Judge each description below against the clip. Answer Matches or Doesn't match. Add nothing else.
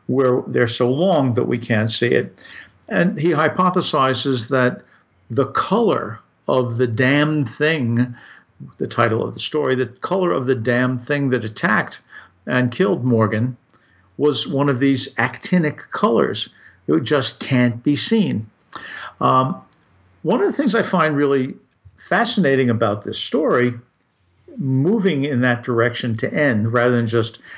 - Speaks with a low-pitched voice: Matches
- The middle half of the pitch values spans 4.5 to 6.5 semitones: Doesn't match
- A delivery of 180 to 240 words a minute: Doesn't match